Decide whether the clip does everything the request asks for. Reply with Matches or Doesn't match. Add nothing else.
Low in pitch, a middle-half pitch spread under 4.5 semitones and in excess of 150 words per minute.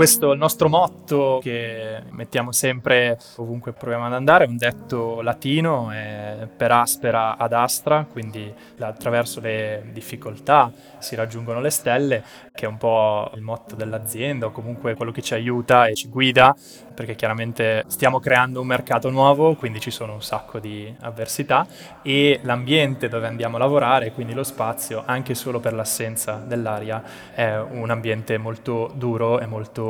Matches